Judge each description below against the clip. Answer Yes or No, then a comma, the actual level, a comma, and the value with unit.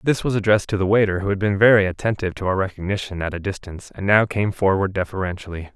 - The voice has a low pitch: Yes, very low, 95 Hz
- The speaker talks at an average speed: No, fast, 230 wpm